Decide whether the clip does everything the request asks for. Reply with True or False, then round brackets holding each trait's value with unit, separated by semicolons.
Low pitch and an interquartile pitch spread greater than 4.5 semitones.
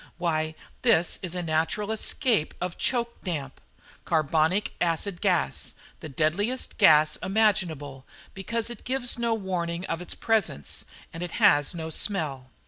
False (175 Hz; 5.1 semitones)